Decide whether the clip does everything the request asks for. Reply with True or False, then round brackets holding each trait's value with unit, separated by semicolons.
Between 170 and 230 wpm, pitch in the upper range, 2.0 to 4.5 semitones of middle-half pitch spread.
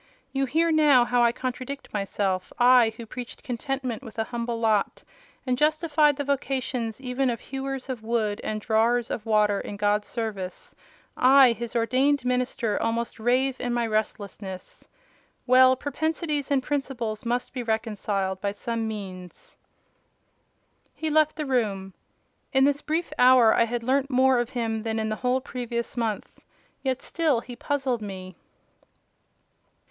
False (150 wpm; 245 Hz; 3.4 semitones)